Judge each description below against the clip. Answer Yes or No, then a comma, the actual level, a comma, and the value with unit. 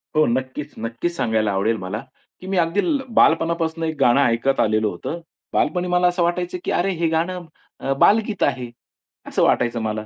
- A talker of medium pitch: Yes, medium, 160 Hz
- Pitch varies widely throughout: Yes, wide, 7.3 semitones